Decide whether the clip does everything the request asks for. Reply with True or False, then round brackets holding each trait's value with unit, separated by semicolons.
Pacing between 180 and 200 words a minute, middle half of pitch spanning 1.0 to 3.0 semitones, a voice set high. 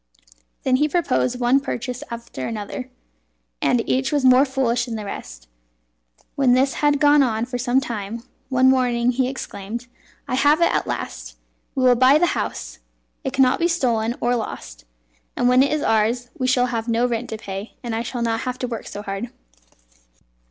True (185 wpm; 2.5 semitones; 245 Hz)